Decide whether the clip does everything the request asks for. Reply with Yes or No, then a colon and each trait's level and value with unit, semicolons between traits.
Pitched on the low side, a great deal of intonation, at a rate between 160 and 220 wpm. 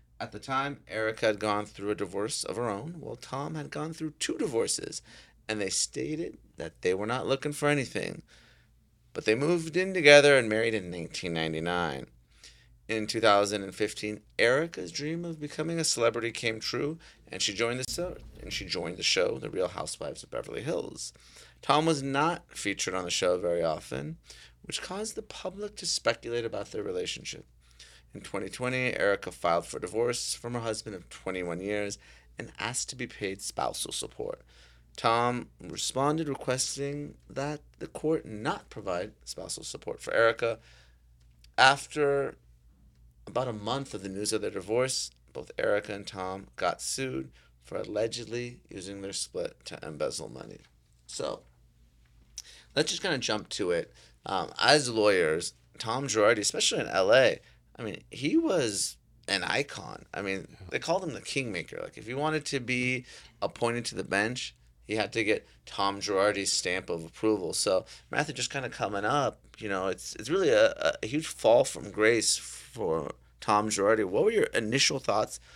Yes: low, 110 Hz; wide, 8.4 semitones; average, 170 wpm